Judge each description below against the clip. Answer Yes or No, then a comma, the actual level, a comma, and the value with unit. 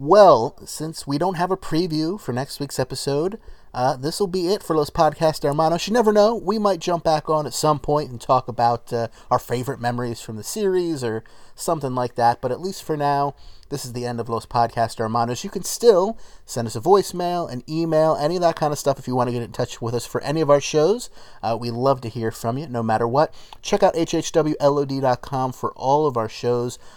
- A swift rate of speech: Yes, fast, 235 wpm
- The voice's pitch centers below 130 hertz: No, medium, 140 Hz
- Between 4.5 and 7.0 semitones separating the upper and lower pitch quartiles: Yes, average, 5.0 semitones